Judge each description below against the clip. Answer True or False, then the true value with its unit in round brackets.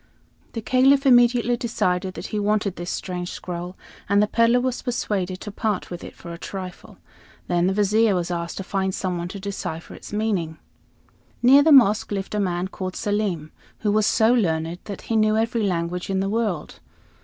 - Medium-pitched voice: False (200 Hz)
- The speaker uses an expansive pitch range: False (3.8 semitones)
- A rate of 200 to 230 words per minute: False (190 wpm)